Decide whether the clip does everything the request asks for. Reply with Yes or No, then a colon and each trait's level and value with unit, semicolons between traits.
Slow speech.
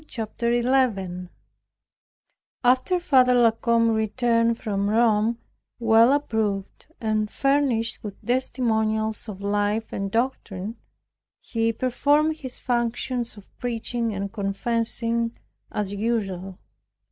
Yes: slow, 100 wpm